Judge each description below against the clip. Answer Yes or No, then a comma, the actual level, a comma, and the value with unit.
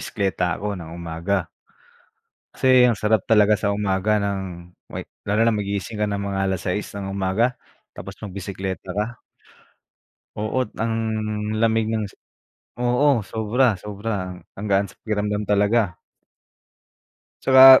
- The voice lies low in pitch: Yes, low, 105 Hz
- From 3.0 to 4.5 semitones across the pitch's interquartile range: No, narrow, 2.5 semitones